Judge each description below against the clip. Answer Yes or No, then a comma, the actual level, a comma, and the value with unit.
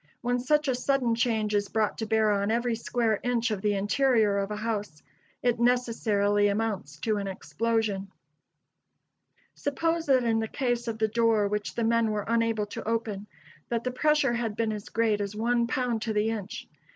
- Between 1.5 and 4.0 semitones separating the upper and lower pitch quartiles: Yes, narrow, 2.4 semitones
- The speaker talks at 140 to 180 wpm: No, average, 190 wpm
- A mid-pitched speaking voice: No, high, 225 Hz